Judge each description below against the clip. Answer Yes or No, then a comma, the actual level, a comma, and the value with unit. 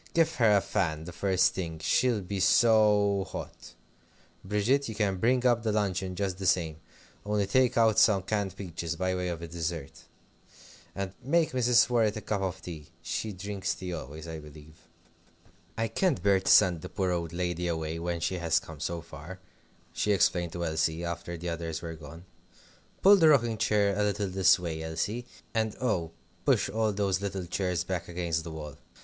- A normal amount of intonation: Yes, average, 3.9 semitones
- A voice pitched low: Yes, very low, 95 Hz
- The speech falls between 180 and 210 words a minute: Yes, average, 190 wpm